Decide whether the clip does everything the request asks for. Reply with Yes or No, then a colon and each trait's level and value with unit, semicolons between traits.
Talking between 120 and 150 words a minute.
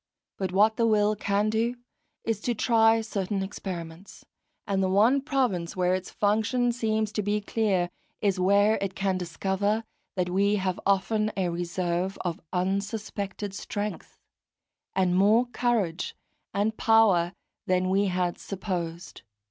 Yes: average, 140 wpm